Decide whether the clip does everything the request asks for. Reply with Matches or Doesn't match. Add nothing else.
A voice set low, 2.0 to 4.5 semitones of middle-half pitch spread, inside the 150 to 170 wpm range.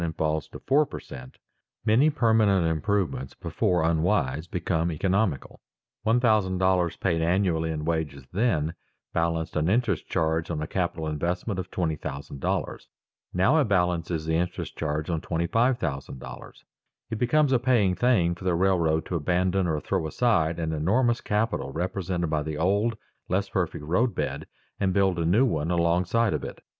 Matches